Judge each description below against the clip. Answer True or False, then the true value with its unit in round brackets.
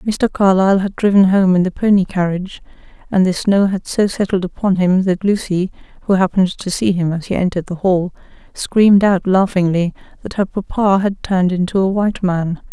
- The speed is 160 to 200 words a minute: True (195 wpm)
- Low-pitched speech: False (190 Hz)